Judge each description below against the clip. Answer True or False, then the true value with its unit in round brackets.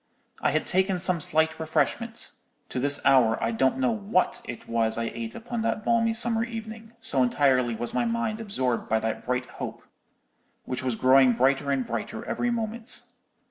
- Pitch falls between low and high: True (145 Hz)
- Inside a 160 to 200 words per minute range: True (175 wpm)